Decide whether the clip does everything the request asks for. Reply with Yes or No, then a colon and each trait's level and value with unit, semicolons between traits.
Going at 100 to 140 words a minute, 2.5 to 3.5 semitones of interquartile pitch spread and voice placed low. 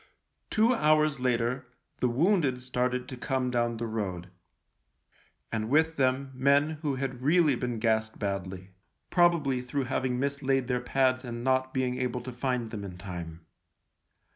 No: average, 155 wpm; average, 2.8 semitones; low, 125 Hz